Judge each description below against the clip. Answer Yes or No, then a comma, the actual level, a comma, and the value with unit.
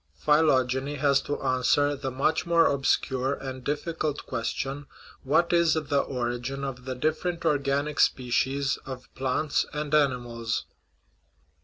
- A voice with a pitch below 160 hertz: Yes, medium, 140 Hz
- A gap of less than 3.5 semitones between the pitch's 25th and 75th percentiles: Yes, narrow, 2.5 semitones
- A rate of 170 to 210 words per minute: No, slow, 135 wpm